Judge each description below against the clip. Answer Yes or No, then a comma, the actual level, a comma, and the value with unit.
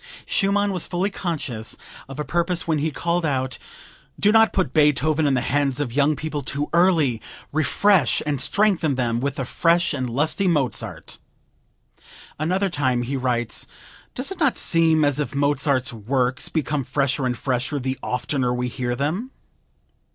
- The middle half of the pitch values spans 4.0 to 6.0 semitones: Yes, average, 4.6 semitones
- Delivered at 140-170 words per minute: Yes, average, 160 wpm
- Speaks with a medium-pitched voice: Yes, medium, 145 Hz